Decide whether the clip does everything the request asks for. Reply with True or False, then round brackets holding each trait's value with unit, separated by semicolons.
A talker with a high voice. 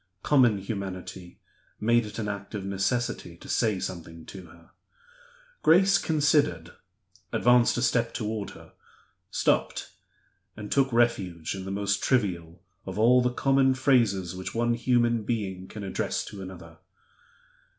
False (105 Hz)